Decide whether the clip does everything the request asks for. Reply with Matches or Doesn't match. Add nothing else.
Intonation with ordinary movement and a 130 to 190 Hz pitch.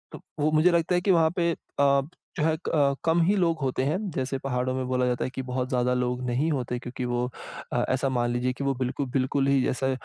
Matches